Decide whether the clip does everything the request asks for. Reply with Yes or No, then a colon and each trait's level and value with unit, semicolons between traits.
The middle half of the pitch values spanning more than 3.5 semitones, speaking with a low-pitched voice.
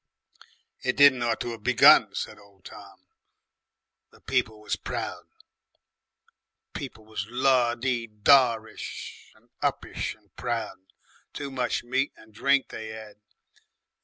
No: average, 2.9 semitones; low, 120 Hz